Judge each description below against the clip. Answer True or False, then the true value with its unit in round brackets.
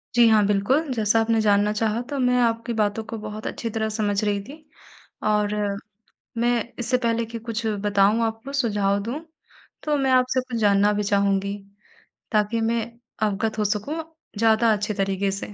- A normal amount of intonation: False (2.2 semitones)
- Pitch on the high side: True (220 Hz)